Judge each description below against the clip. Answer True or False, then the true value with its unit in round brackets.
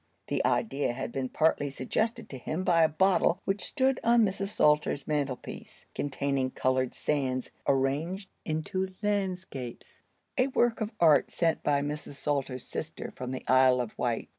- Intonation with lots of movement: True (6.2 semitones)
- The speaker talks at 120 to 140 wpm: False (155 wpm)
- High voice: False (150 Hz)